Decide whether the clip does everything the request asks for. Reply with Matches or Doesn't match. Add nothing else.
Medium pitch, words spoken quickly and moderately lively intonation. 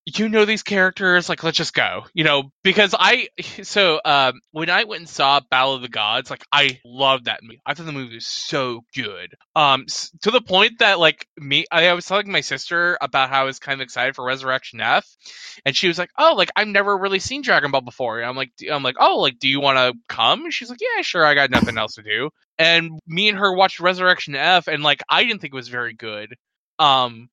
Doesn't match